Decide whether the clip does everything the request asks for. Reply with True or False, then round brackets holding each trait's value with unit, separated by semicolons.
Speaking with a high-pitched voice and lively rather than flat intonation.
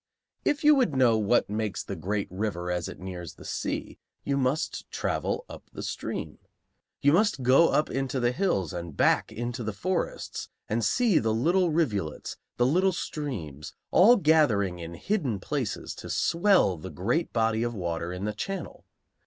False (120 Hz; 9.0 semitones)